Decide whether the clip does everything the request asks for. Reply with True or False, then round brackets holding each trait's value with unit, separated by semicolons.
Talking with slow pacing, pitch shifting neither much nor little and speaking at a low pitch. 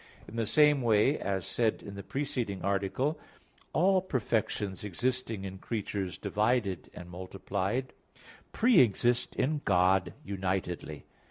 True (120 wpm; 5.0 semitones; 105 Hz)